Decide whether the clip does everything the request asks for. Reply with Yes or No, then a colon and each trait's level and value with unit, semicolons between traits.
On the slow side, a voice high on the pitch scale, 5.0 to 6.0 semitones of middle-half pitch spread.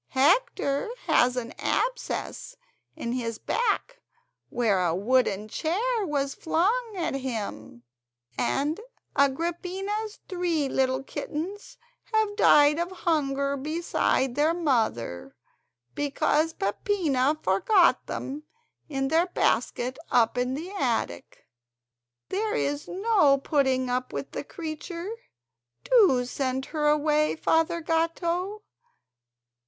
Yes: slow, 105 wpm; very high, 295 Hz; wide, 5.6 semitones